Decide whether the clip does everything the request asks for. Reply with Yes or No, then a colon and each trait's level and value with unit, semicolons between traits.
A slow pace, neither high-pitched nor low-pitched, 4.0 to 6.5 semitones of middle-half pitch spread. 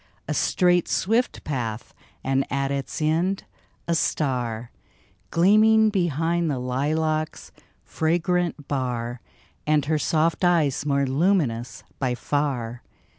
Yes: slow, 115 wpm; medium, 150 Hz; average, 4.7 semitones